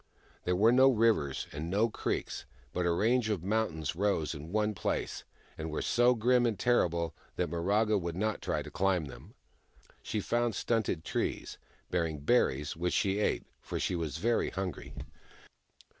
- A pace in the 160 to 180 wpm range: Yes, average, 165 wpm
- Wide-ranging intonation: No, average, 5.0 semitones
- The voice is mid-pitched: No, very low, 95 Hz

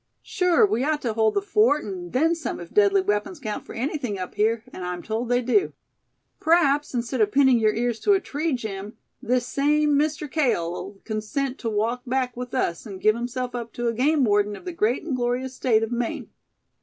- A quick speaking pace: Yes, fast, 210 wpm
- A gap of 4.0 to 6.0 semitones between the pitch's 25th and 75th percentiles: Yes, average, 4.8 semitones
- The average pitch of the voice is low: No, high, 245 Hz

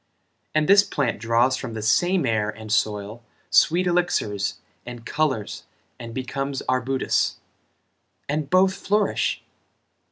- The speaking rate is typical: No, slow, 120 wpm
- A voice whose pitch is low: Yes, low, 130 Hz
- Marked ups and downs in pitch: Yes, wide, 6.6 semitones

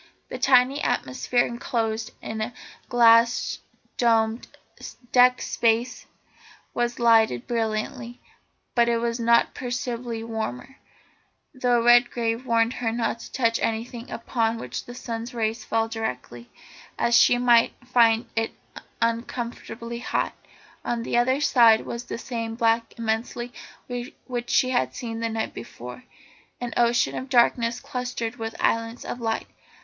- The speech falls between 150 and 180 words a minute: No, slow, 135 wpm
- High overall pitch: Yes, high, 235 Hz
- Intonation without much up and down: Yes, narrow, 1.3 semitones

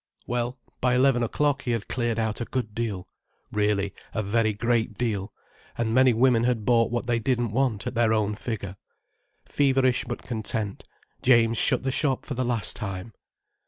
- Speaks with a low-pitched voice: Yes, low, 115 Hz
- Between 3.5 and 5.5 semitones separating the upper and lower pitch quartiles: No, narrow, 2.4 semitones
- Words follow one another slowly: No, average, 165 wpm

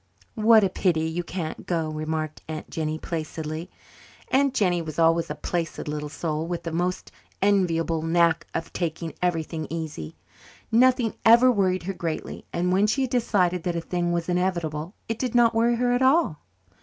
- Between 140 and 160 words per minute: No, average, 175 wpm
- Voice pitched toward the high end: No, medium, 175 Hz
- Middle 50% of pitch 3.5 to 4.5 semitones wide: Yes, average, 4.1 semitones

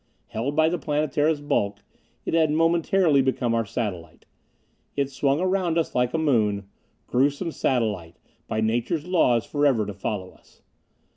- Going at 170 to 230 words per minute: No, average, 145 wpm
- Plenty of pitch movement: Yes, wide, 6.3 semitones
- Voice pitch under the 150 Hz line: Yes, low, 135 Hz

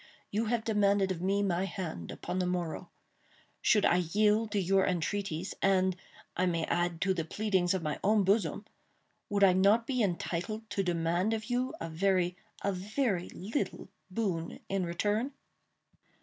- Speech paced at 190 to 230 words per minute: No, average, 150 wpm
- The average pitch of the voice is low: No, high, 190 Hz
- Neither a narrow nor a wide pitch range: Yes, average, 3.0 semitones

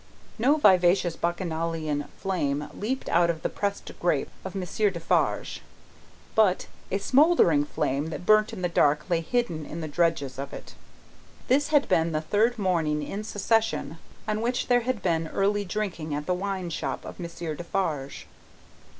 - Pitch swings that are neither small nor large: Yes, average, 4.9 semitones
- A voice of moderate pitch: Yes, medium, 175 Hz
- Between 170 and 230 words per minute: No, average, 160 wpm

